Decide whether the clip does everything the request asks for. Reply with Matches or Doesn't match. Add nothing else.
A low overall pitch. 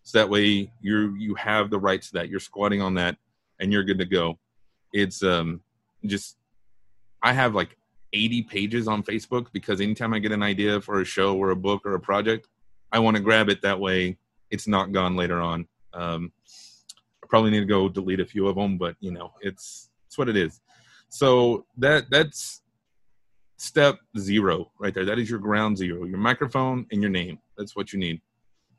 Matches